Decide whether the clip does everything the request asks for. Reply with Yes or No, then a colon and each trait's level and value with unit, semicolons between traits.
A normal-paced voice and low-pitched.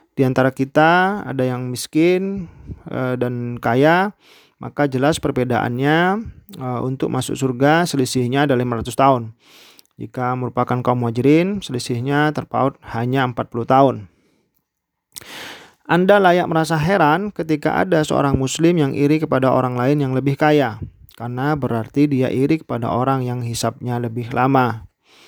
Yes: average, 125 wpm; low, 130 Hz